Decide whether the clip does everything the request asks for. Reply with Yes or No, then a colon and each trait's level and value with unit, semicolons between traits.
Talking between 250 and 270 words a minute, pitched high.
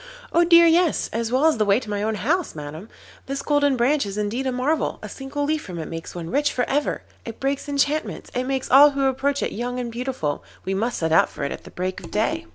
Yes: fast, 255 wpm; very high, 255 Hz